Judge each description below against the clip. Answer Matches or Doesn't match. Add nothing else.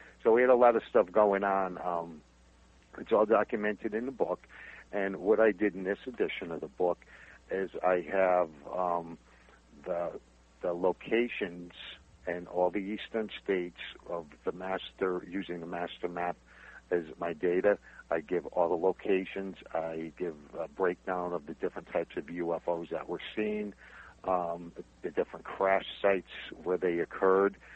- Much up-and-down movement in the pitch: Doesn't match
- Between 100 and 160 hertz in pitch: Doesn't match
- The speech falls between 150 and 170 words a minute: Matches